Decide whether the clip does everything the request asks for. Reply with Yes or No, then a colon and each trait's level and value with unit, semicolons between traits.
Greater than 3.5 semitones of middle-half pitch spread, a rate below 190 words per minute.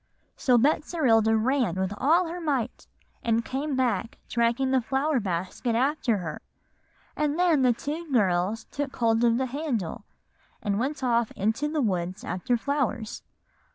Yes: average, 4.3 semitones; average, 150 wpm